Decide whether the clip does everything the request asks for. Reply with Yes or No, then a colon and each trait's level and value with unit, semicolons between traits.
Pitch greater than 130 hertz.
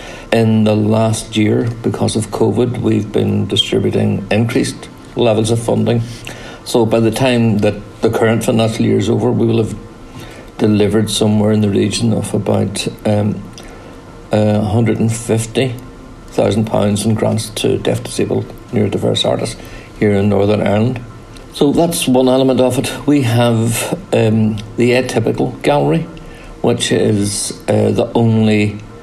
No: low, 115 Hz